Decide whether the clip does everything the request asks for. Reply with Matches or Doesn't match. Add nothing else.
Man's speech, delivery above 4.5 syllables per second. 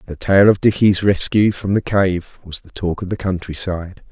Matches